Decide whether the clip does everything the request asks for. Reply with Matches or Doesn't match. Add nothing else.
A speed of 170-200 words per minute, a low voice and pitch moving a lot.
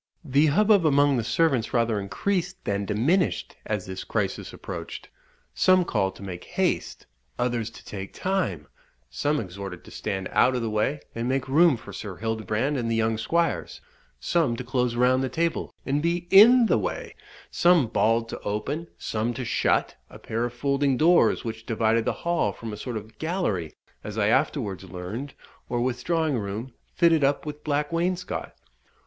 Matches